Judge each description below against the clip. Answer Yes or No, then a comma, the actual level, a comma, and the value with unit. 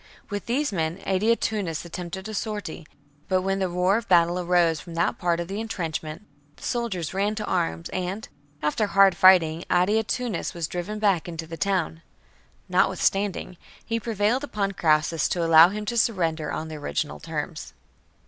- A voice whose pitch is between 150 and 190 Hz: Yes, medium, 185 Hz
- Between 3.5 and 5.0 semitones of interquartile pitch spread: Yes, average, 3.9 semitones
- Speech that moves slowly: No, average, 170 wpm